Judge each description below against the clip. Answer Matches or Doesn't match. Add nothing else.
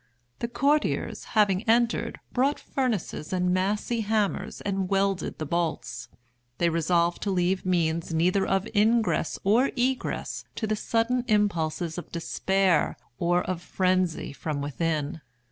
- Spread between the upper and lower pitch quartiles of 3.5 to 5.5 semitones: Matches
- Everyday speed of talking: Doesn't match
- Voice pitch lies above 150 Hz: Matches